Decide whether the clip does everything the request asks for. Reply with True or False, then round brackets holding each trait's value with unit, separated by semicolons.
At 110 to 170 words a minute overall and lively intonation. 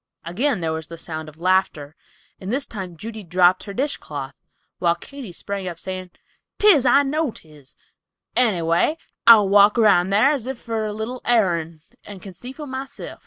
False (180 wpm; 6.3 semitones)